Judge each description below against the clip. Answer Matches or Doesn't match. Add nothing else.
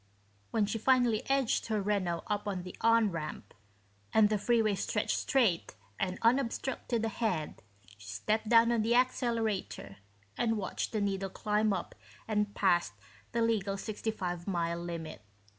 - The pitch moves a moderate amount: Matches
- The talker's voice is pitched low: Doesn't match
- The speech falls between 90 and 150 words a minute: Matches